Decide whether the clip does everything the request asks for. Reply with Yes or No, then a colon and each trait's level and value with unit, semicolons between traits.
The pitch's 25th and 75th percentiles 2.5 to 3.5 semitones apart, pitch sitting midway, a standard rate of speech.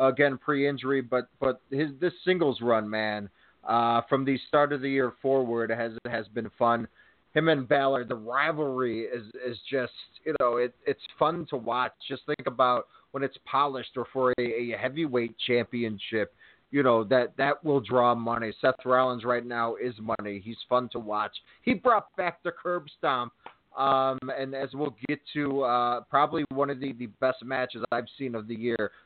No: average, 2.9 semitones; low, 130 Hz; average, 190 wpm